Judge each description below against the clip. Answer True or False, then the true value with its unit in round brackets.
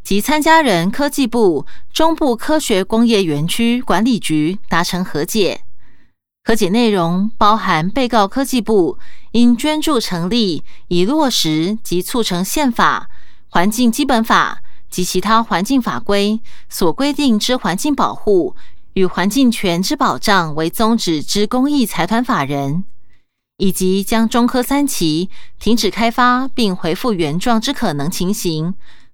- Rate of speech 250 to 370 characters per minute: False (215 characters per minute)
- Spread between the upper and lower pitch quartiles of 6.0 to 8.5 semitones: False (5.6 semitones)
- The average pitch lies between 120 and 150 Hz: False (215 Hz)